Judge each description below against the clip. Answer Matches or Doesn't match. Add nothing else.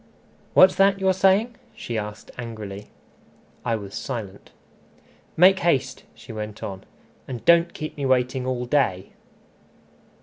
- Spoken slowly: Matches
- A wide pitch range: Matches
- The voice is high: Doesn't match